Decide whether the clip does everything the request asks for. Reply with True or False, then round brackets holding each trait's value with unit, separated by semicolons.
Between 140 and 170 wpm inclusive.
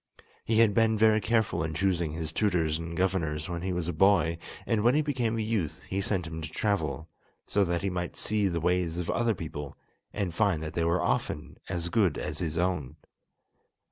False (205 wpm)